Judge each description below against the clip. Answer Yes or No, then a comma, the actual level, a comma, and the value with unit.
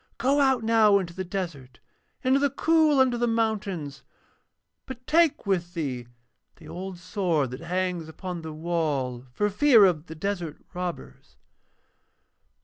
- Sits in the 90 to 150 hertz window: No, medium, 185 Hz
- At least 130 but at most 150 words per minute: Yes, average, 140 wpm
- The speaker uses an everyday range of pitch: No, wide, 6.0 semitones